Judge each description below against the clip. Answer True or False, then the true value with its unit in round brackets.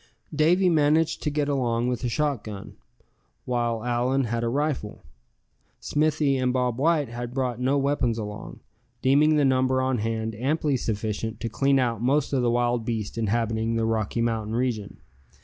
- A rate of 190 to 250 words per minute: False (165 wpm)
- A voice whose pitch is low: True (125 Hz)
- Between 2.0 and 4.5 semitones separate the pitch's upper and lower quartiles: True (3.5 semitones)